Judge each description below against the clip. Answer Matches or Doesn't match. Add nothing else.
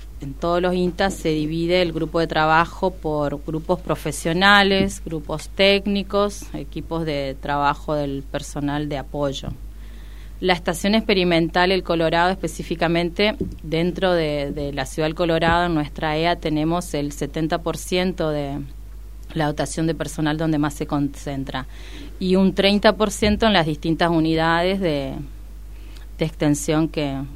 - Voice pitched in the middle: Matches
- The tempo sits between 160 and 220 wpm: Doesn't match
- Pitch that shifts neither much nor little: Matches